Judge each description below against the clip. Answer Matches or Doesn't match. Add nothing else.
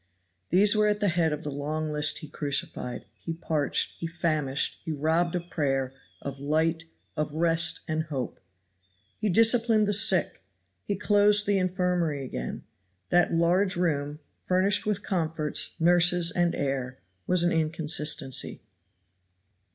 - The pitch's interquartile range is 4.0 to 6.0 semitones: Doesn't match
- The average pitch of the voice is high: Doesn't match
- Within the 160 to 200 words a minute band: Doesn't match